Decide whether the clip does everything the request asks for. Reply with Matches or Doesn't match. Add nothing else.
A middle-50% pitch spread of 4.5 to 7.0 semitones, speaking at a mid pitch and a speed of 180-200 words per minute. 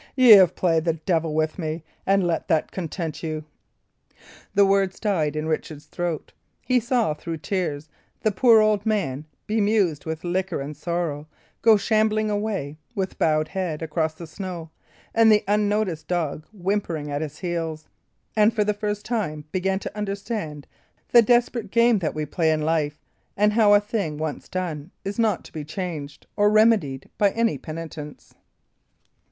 Doesn't match